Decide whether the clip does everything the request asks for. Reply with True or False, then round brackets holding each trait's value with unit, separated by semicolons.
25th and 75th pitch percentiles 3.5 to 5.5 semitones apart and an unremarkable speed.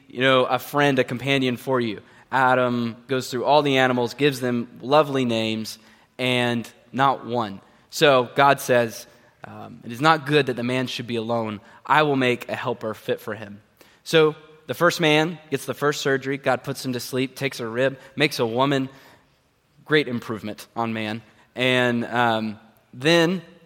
False (2.8 semitones; 175 wpm)